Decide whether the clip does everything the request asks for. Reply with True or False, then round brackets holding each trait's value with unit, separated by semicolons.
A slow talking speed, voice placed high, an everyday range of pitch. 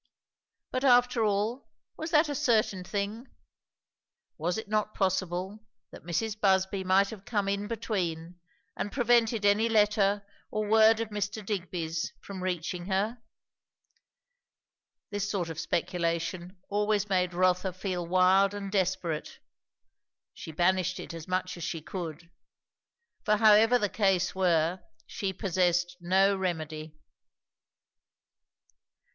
True (125 wpm; 195 Hz; 3.0 semitones)